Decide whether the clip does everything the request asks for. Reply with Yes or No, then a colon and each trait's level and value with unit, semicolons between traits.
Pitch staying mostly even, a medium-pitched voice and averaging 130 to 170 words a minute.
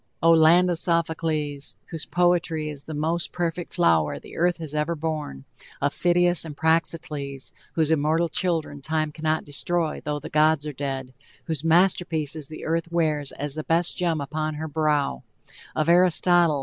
Yes: narrow, 2.2 semitones; medium, 160 Hz; average, 160 wpm